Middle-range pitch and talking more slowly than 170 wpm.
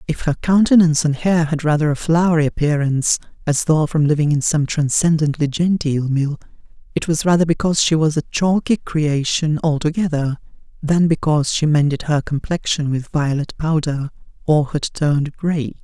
Yes: medium, 155 Hz; average, 160 wpm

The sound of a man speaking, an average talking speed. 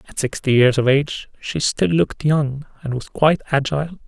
Yes: male; average, 190 wpm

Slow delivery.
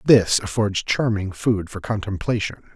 Yes: slow, 130 wpm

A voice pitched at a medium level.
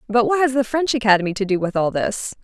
No: high, 230 Hz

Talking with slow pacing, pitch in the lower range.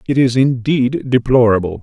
Yes: slow, 130 wpm; low, 125 Hz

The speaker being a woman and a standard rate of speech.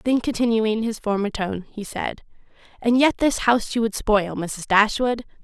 Yes: female; average, 175 wpm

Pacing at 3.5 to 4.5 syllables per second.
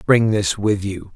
Yes: 4.0 syllables/s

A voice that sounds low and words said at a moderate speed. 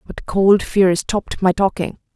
No: high, 190 Hz; average, 165 wpm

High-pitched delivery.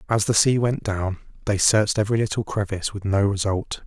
No: low, 105 Hz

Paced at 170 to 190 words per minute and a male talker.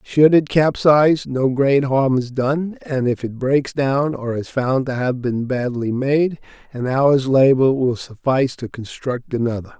Yes: average, 180 wpm; male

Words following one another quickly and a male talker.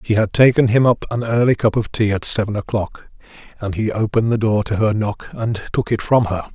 Yes: fast, 240 wpm; male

